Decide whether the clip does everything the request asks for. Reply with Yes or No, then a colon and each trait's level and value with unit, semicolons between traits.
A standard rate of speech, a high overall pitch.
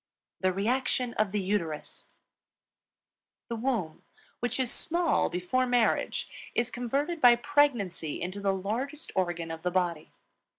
No: slow, 130 wpm; high, 220 Hz